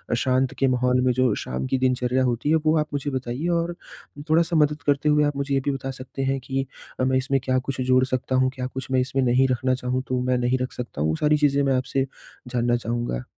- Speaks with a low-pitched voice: Yes, low, 130 Hz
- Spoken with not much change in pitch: Yes, narrow, 1.7 semitones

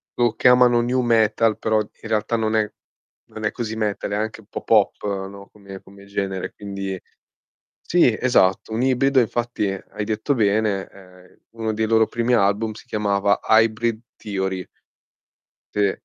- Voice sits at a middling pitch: No, low, 110 Hz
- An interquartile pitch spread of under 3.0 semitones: Yes, narrow, 2.4 semitones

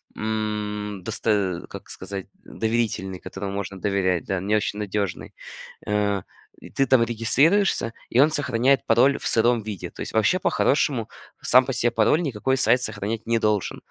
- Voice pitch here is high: No, low, 110 Hz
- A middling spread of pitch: Yes, average, 3.2 semitones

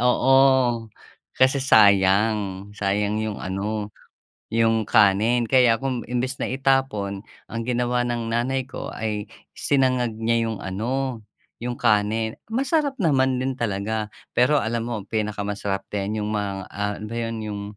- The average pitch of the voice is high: No, low, 115 Hz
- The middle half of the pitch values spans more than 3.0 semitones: Yes, average, 3.4 semitones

